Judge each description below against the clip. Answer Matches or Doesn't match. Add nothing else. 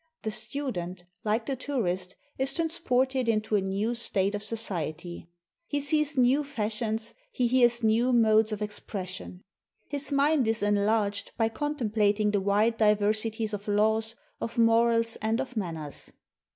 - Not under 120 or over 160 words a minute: Matches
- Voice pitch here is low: Doesn't match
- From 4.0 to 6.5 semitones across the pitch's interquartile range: Doesn't match